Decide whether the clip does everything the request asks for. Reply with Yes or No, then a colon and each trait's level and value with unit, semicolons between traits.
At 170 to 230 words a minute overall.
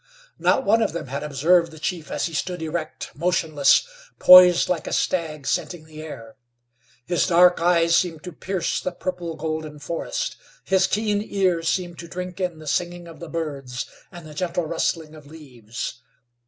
Yes: average, 175 wpm